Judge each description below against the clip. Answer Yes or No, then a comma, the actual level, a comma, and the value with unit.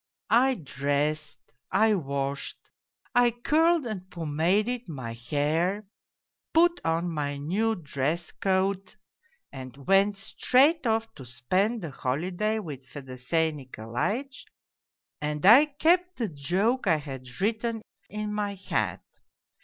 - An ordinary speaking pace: No, slow, 115 wpm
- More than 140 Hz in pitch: Yes, medium, 185 Hz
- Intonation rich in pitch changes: Yes, wide, 7.6 semitones